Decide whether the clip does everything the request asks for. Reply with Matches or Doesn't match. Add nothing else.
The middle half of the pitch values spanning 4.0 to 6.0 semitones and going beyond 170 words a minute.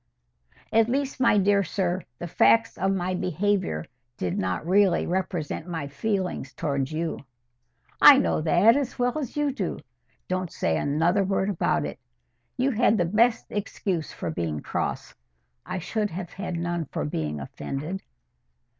Doesn't match